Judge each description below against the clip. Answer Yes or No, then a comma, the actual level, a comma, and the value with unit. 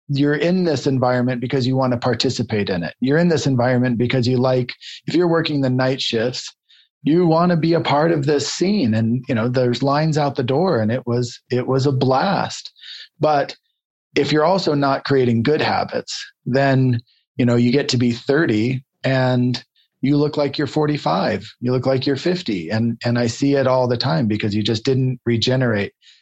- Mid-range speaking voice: No, low, 130 Hz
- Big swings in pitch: No, average, 3.0 semitones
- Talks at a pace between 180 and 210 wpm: Yes, average, 200 wpm